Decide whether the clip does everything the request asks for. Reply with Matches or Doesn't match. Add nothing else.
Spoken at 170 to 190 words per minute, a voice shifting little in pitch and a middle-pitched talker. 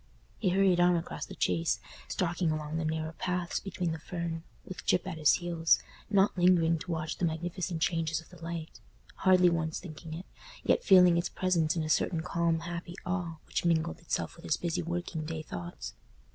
Matches